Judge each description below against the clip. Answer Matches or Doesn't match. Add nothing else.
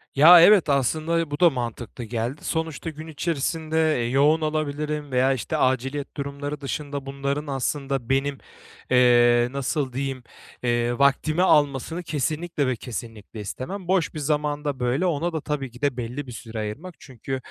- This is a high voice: Doesn't match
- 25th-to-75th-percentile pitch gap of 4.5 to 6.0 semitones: Doesn't match